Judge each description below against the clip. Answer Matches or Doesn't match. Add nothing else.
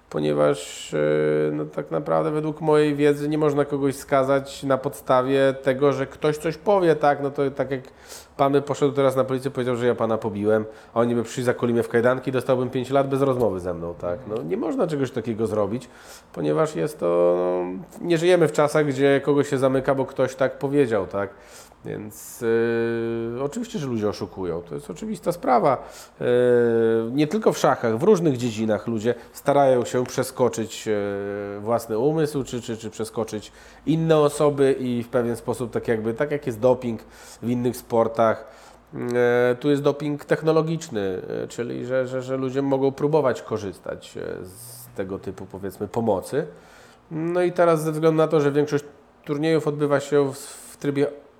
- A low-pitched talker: Matches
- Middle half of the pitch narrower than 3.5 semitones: Doesn't match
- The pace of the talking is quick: Matches